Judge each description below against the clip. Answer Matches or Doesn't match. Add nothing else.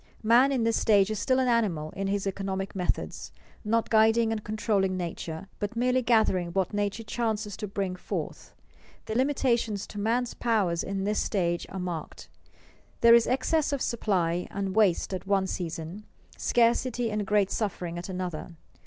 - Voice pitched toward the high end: Matches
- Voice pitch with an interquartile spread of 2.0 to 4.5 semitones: Matches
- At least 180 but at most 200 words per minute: Doesn't match